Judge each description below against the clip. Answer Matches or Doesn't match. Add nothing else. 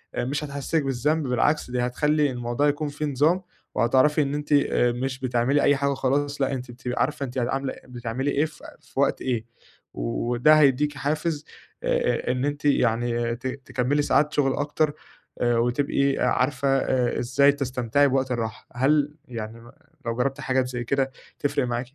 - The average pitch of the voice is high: Doesn't match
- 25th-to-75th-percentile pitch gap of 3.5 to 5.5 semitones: Doesn't match